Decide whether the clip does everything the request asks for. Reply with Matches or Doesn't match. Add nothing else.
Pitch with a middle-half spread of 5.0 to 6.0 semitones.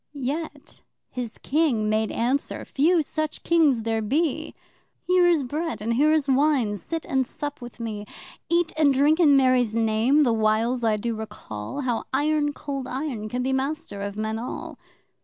Matches